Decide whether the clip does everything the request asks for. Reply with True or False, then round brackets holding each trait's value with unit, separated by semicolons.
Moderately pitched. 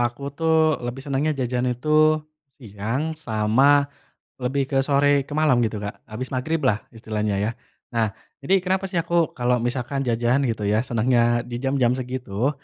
False (125 Hz)